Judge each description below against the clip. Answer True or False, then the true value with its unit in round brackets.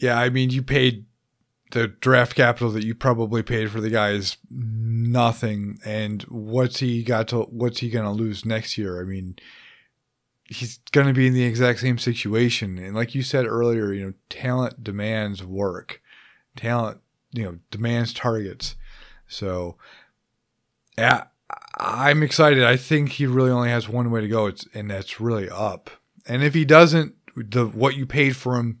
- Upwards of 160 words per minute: True (170 wpm)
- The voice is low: True (120 Hz)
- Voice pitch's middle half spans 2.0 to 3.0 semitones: True (2.7 semitones)